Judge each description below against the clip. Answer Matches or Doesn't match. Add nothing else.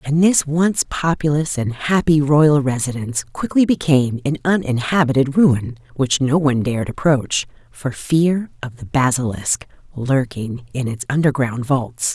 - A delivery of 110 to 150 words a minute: Matches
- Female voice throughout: Matches